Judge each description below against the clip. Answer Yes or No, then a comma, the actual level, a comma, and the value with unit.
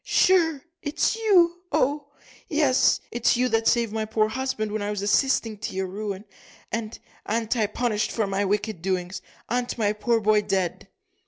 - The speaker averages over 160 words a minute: Yes, average, 170 wpm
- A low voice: No, high, 220 Hz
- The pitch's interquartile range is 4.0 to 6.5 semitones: No, average, 3.6 semitones